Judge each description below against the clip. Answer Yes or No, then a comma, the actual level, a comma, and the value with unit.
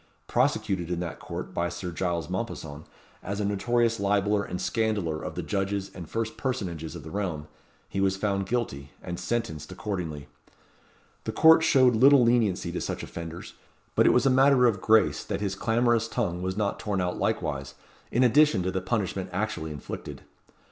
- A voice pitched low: Yes, low, 100 Hz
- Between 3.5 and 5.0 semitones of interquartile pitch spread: Yes, average, 4.7 semitones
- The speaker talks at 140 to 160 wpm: No, average, 175 wpm